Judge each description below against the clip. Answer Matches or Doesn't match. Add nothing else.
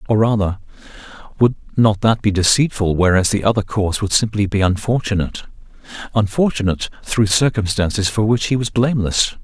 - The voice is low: Matches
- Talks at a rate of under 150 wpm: Matches